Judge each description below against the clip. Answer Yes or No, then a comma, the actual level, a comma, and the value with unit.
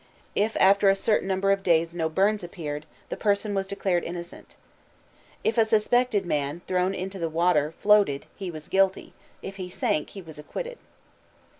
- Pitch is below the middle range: No, high, 190 Hz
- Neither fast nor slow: Yes, average, 170 wpm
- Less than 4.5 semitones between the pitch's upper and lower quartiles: Yes, average, 3.2 semitones